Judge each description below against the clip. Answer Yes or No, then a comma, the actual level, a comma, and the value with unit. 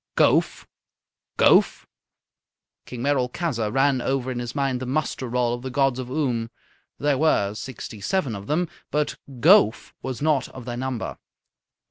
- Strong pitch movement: No, average, 2.9 semitones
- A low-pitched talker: Yes, low, 130 Hz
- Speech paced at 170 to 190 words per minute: No, average, 150 wpm